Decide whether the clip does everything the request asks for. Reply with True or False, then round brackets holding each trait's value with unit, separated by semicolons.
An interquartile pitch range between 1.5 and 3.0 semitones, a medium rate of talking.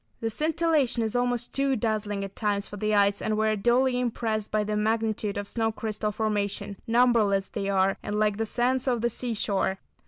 True (2.7 semitones; 195 wpm)